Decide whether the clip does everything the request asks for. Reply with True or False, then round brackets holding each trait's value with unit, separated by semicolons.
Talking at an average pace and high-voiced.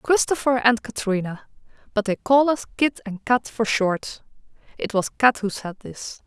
True (170 wpm; 230 Hz)